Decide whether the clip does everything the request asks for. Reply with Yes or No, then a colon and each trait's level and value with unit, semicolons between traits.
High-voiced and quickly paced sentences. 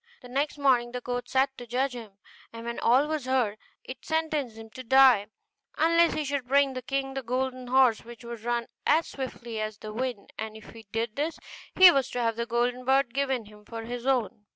Yes: very high, 250 Hz; fast, 220 wpm